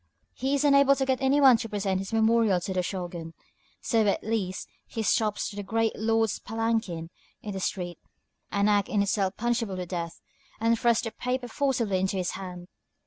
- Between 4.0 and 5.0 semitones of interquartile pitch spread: No, average, 3.5 semitones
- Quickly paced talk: No, average, 190 wpm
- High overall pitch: Yes, high, 215 Hz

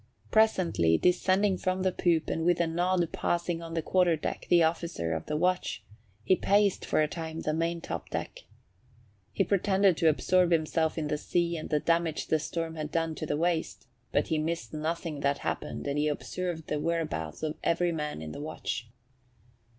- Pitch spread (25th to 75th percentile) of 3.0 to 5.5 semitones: No, narrow, 2.5 semitones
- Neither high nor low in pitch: Yes, medium, 165 Hz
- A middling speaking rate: Yes, average, 190 wpm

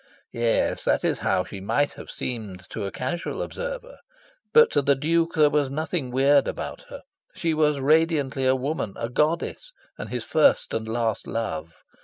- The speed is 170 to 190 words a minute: Yes, average, 175 wpm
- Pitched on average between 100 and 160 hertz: Yes, medium, 140 Hz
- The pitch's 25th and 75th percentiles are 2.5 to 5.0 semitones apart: No, wide, 5.4 semitones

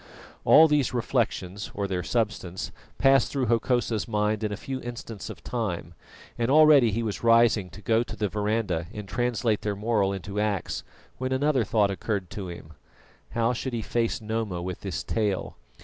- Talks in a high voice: No, low, 110 Hz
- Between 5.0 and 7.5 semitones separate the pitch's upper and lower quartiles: No, average, 3.1 semitones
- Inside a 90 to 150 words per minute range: No, average, 175 wpm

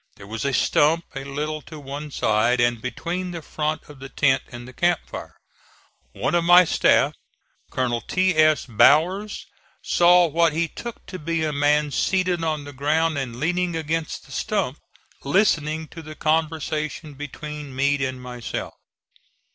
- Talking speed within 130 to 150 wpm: No, average, 160 wpm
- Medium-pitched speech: Yes, medium, 155 Hz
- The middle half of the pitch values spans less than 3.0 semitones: No, average, 3.4 semitones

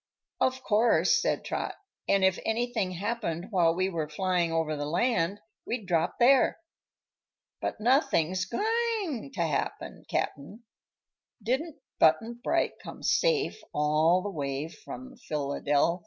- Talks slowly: Yes, slow, 125 wpm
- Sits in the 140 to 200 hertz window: Yes, high, 190 Hz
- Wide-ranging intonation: Yes, wide, 7.1 semitones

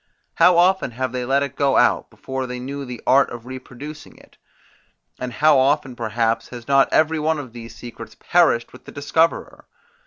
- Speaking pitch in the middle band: No, low, 130 Hz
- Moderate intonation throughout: Yes, average, 3.3 semitones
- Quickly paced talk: No, average, 185 wpm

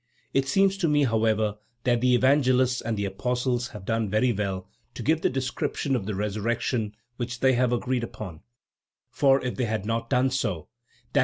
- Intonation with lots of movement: No, average, 3.3 semitones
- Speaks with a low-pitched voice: Yes, low, 120 Hz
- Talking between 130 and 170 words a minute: No, average, 185 wpm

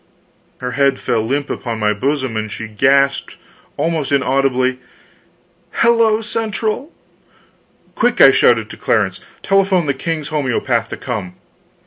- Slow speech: Yes, slow, 125 wpm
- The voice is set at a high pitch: No, low, 135 Hz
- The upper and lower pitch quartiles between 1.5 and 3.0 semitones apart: No, average, 5.3 semitones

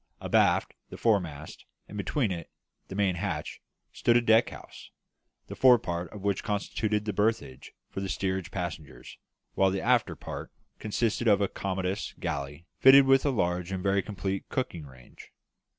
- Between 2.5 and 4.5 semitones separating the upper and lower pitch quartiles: Yes, average, 3.8 semitones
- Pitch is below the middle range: Yes, very low, 95 Hz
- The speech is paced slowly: No, average, 165 wpm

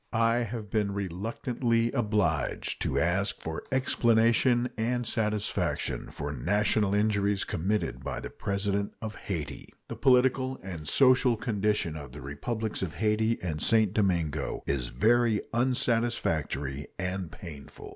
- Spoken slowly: Yes, slow, 125 wpm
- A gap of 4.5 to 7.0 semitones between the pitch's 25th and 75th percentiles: Yes, average, 4.9 semitones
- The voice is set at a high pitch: No, low, 105 Hz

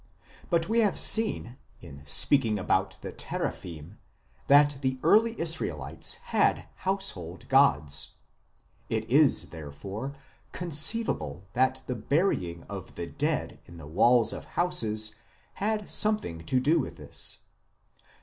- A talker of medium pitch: No, low, 130 Hz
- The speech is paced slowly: Yes, slow, 120 wpm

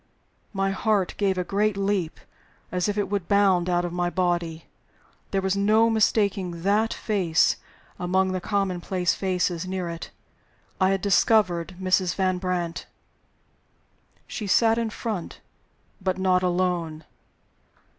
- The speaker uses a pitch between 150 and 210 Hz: Yes, medium, 185 Hz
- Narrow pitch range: Yes, narrow, 2.2 semitones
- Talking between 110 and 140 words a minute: Yes, slow, 135 wpm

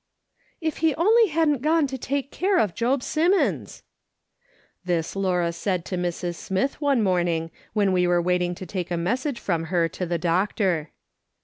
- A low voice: No, high, 190 Hz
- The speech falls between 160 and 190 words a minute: Yes, average, 175 wpm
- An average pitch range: No, wide, 8.1 semitones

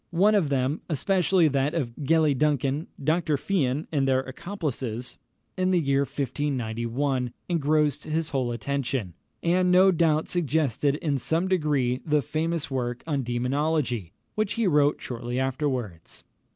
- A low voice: No, medium, 145 Hz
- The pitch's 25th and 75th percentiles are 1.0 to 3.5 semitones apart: No, average, 3.9 semitones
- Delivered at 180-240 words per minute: No, average, 140 wpm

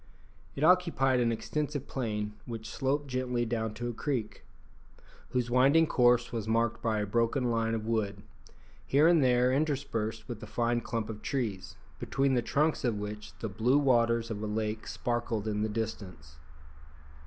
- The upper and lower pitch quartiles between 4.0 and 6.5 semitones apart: No, average, 3.1 semitones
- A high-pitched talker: No, low, 115 Hz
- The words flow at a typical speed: Yes, average, 165 wpm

